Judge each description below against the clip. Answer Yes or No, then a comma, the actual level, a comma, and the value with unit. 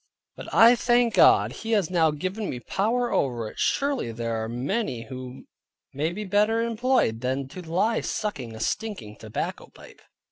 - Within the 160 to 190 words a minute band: Yes, average, 170 wpm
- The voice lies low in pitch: No, medium, 180 Hz